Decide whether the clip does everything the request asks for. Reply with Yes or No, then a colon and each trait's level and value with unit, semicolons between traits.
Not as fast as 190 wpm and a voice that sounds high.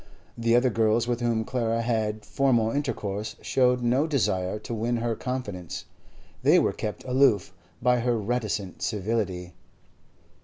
No: average, 140 wpm; low, 115 Hz